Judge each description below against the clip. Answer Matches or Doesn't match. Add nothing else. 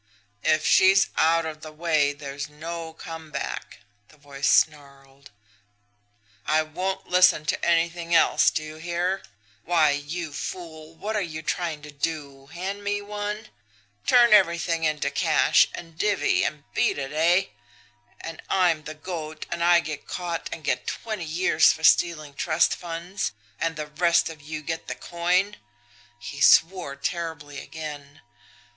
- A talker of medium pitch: Matches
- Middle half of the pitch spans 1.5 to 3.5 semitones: Matches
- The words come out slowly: Doesn't match